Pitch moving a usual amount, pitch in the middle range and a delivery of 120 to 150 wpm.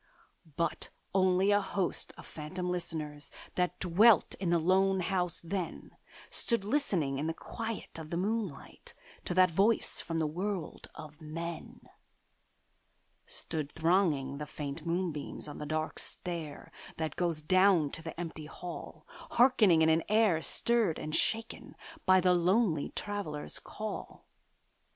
Yes: average, 3.6 semitones; medium, 175 Hz; average, 140 wpm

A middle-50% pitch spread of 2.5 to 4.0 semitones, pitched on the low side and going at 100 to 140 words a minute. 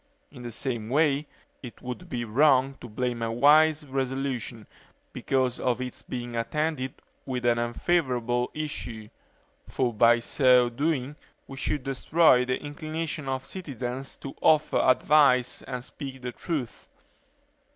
Yes: average, 3.1 semitones; low, 130 Hz; slow, 135 wpm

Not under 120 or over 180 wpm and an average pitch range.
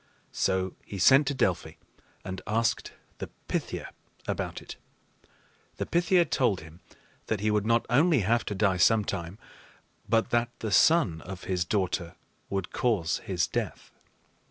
Yes: average, 150 wpm; average, 4.3 semitones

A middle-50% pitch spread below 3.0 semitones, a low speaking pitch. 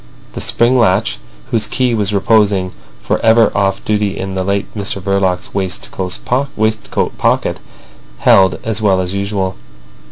Yes: narrow, 2.4 semitones; low, 100 Hz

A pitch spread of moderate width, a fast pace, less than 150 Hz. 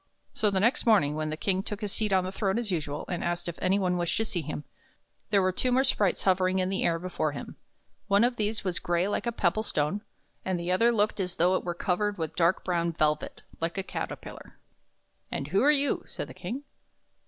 No: average, 3.4 semitones; fast, 240 wpm; medium, 185 Hz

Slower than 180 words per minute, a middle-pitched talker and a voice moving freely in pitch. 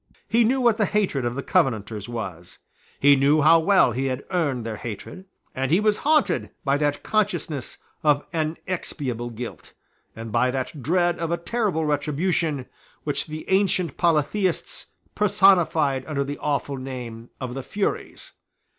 Yes: average, 155 wpm; medium, 150 Hz; wide, 6.0 semitones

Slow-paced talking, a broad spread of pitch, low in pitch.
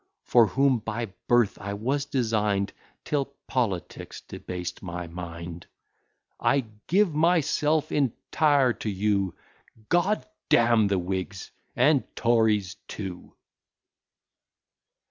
Yes: slow, 105 wpm; wide, 6.4 semitones; low, 115 Hz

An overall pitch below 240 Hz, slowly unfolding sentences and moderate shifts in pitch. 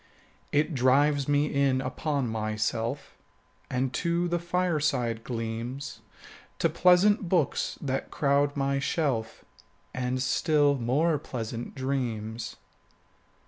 Yes: medium, 140 Hz; slow, 105 wpm; average, 3.7 semitones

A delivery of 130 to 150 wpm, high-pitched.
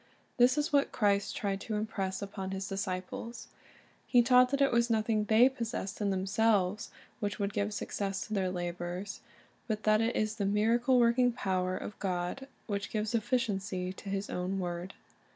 No: average, 185 wpm; high, 205 Hz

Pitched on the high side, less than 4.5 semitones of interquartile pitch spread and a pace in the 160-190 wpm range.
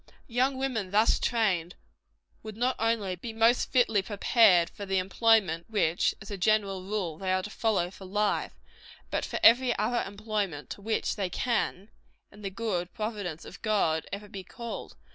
Yes: high, 205 Hz; average, 3.3 semitones; average, 170 wpm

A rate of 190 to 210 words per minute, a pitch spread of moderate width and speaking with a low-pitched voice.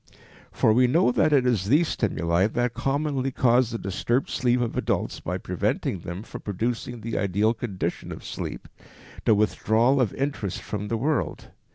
No: average, 170 wpm; average, 3.6 semitones; low, 115 Hz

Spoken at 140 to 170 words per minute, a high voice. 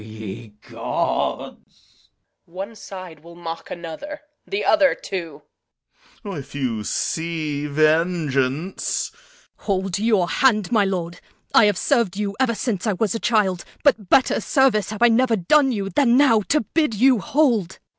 Yes: average, 160 wpm; high, 195 Hz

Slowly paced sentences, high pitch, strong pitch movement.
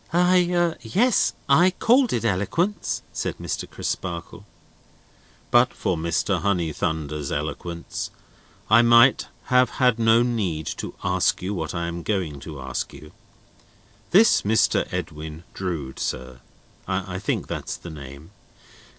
No: slow, 125 wpm; very low, 95 Hz; wide, 7.9 semitones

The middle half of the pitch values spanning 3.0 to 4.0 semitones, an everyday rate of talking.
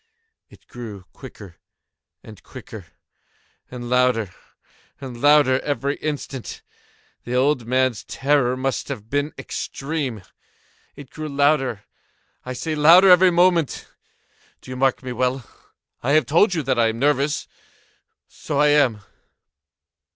No: average, 3.3 semitones; slow, 125 wpm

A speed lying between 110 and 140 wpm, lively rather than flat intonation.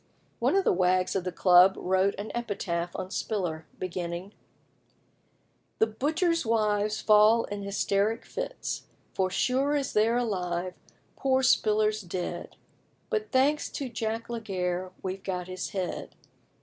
No: slow, 135 wpm; average, 4.0 semitones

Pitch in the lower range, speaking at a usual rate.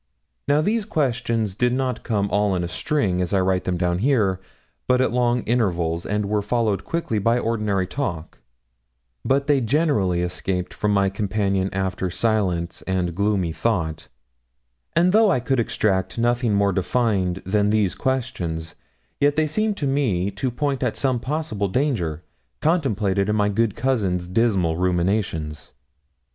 Yes: low, 105 Hz; average, 155 wpm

